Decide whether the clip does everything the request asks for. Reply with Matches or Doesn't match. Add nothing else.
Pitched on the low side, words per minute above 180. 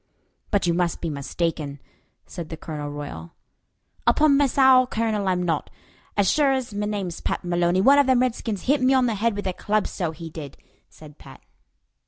Doesn't match